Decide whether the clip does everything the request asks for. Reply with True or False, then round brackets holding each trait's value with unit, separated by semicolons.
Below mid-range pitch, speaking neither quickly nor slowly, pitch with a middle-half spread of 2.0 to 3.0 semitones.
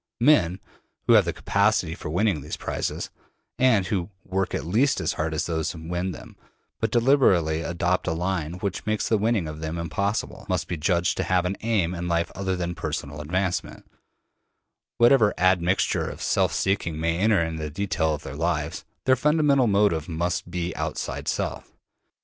False (90 Hz; 180 wpm; 3.6 semitones)